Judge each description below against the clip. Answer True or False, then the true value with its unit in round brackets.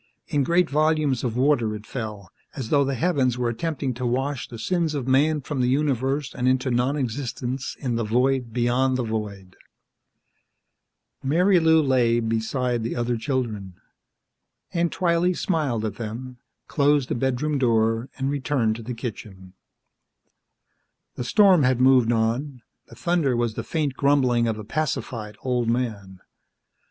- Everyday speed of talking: True (150 wpm)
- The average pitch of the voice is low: True (125 Hz)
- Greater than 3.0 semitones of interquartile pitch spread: True (3.7 semitones)